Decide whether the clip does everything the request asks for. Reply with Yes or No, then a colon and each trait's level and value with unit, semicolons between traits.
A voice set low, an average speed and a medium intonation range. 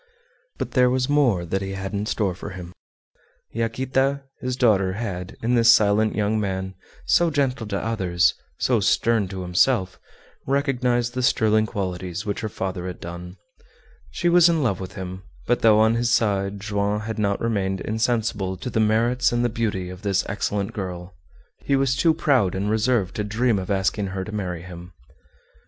Yes: low, 105 Hz; average, 180 wpm; average, 4.0 semitones